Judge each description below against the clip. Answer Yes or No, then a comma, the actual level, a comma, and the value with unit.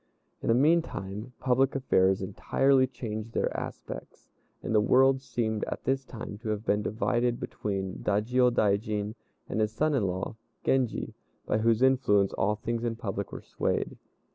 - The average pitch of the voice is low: Yes, low, 115 Hz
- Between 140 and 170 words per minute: Yes, average, 160 wpm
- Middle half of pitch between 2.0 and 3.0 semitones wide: No, average, 3.6 semitones